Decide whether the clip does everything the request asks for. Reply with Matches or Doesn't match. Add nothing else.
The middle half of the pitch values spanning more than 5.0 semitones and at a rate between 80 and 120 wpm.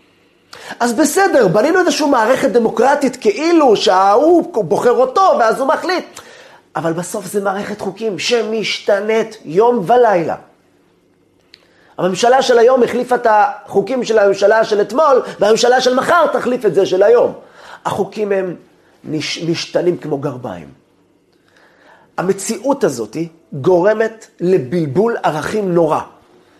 Matches